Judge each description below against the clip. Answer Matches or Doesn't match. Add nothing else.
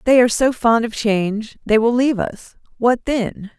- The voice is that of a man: Doesn't match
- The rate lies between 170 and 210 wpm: Matches